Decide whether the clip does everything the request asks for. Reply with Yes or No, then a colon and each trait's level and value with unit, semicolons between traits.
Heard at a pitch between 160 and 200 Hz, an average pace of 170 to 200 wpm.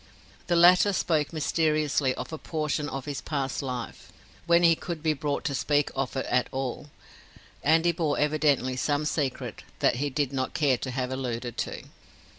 No: medium, 145 Hz; average, 180 wpm